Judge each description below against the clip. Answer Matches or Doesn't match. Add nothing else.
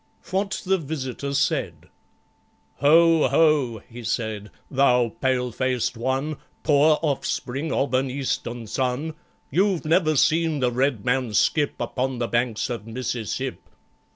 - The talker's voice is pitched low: Matches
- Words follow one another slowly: Matches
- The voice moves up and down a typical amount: Matches